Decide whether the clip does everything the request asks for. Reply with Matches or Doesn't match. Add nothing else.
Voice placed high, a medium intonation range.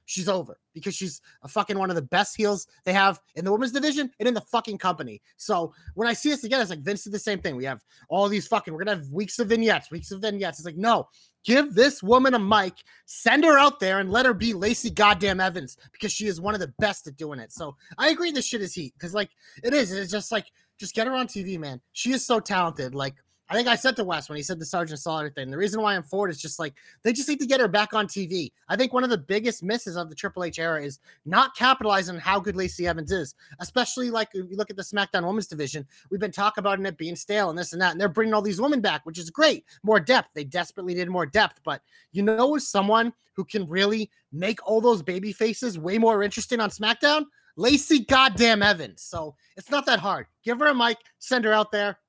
Matches